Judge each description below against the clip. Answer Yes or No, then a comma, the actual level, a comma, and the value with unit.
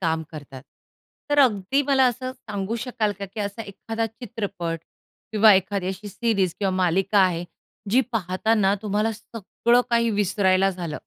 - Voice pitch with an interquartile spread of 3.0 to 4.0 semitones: Yes, average, 3.3 semitones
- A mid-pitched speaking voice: No, high, 205 Hz